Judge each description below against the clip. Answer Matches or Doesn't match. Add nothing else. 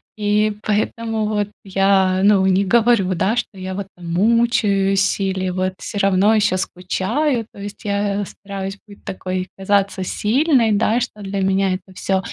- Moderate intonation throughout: Doesn't match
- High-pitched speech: Matches